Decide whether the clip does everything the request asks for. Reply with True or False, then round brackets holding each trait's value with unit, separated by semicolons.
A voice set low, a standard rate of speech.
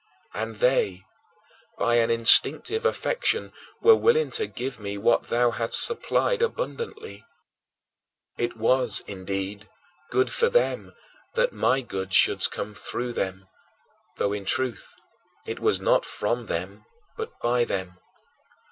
False (120 Hz; 130 wpm)